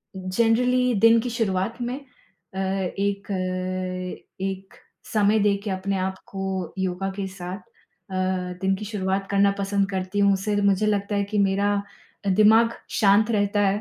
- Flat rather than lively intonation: Yes, narrow, 1.7 semitones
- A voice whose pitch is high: Yes, high, 200 Hz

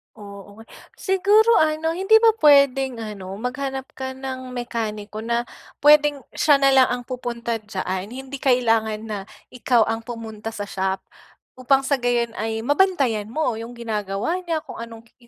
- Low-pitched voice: No, high, 245 Hz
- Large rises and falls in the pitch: No, average, 3.8 semitones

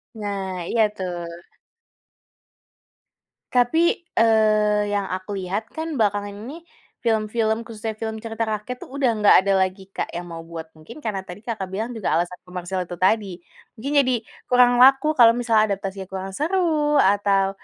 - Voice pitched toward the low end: No, high, 210 Hz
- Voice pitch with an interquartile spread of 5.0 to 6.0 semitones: No, average, 3.6 semitones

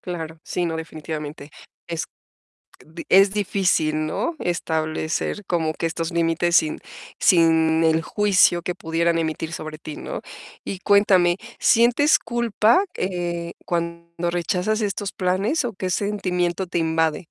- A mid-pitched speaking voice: Yes, medium, 170 Hz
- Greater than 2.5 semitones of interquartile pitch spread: Yes, average, 2.9 semitones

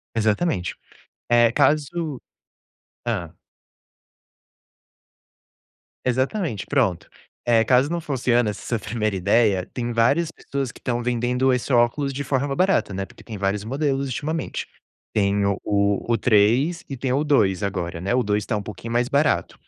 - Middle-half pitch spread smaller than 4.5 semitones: No, average, 4.9 semitones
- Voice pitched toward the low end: Yes, low, 120 Hz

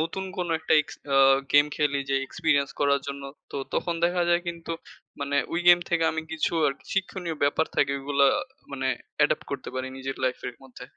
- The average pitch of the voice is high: No, medium, 145 Hz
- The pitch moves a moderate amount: Yes, average, 3.4 semitones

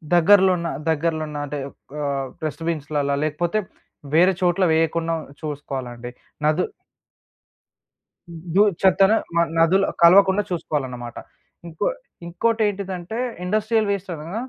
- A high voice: No, medium, 170 Hz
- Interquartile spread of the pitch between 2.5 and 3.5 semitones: No, average, 4.2 semitones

